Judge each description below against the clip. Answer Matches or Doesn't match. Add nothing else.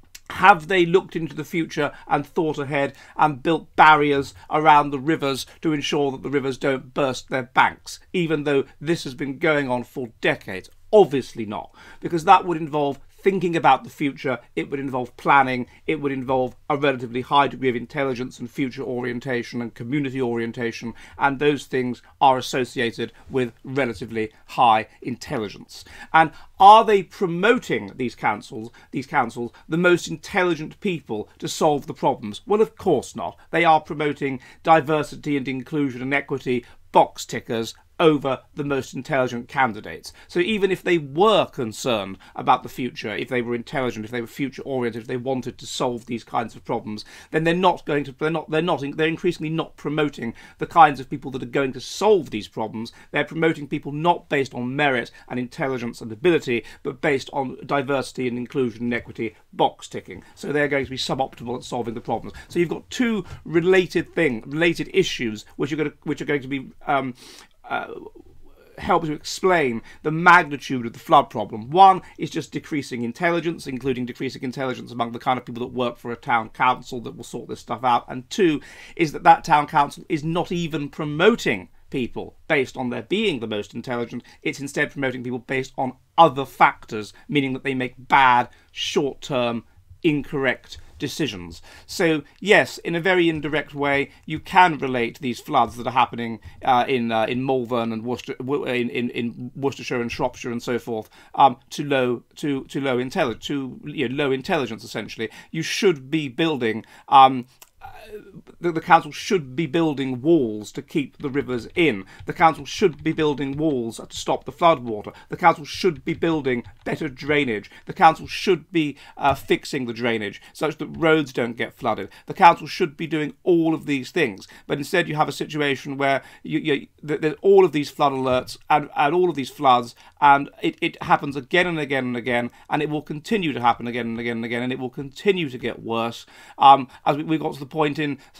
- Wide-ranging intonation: Doesn't match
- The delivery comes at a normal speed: Matches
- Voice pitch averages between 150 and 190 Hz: Doesn't match